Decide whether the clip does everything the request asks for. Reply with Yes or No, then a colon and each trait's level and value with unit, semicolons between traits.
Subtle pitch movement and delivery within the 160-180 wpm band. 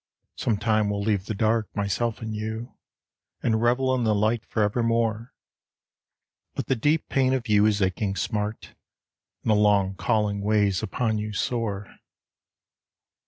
No: narrow, 2.1 semitones; average, 145 wpm